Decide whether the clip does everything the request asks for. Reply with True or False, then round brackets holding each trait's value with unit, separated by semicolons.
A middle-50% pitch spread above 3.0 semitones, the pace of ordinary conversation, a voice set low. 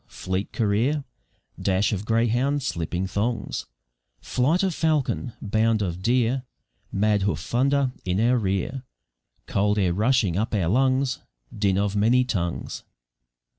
False (4.6 semitones; 130 wpm; 110 Hz)